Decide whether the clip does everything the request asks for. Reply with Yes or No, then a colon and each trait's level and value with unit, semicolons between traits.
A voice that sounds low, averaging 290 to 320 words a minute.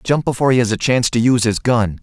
Yes: low, 120 Hz; fast, 295 wpm